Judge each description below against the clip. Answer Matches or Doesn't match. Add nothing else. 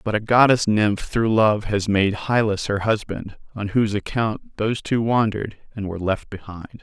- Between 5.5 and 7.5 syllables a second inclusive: Doesn't match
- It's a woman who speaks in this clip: Doesn't match